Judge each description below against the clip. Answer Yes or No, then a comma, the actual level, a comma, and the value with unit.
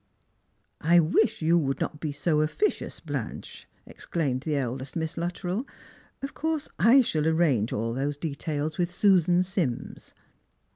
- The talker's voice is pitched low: No, medium, 160 Hz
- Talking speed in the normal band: Yes, average, 150 wpm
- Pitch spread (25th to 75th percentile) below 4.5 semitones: Yes, average, 3.7 semitones